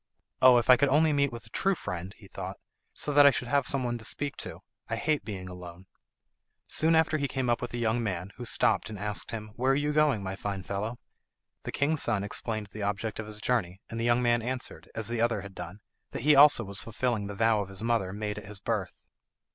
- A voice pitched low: Yes, low, 115 Hz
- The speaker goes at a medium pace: No, fast, 245 wpm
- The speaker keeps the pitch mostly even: No, average, 4.3 semitones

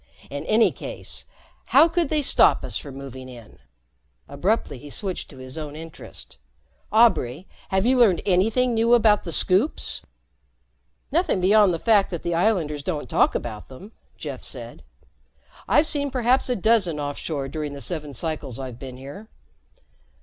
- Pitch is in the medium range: Yes, medium, 180 Hz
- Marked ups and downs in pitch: Yes, wide, 7.9 semitones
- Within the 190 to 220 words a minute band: No, average, 155 wpm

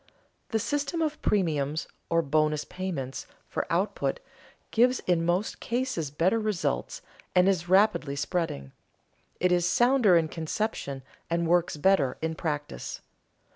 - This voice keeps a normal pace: No, slow, 130 wpm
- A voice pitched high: No, medium, 175 Hz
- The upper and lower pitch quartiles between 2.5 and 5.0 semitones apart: No, wide, 5.4 semitones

